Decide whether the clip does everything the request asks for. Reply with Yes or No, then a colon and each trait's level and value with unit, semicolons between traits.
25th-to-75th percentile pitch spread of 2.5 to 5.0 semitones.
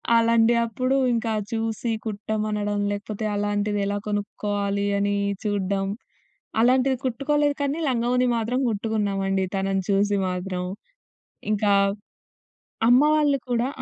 Yes: average, 2.9 semitones